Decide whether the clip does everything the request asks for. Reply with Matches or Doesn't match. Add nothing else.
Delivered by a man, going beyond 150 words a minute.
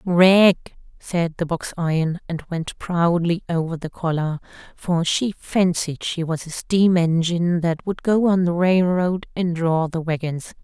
Doesn't match